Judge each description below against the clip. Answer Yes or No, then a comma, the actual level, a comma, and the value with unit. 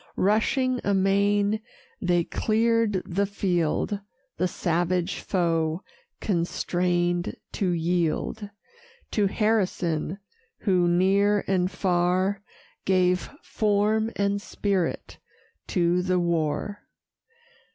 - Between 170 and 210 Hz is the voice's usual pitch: Yes, medium, 185 Hz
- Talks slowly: Yes, slow, 85 wpm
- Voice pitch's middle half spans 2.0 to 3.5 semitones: Yes, average, 2.7 semitones